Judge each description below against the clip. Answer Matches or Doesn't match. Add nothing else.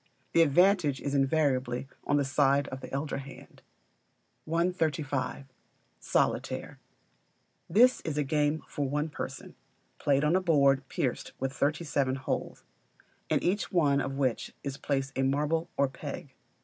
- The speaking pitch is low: Doesn't match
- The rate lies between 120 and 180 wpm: Matches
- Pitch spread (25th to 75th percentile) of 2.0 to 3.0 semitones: Matches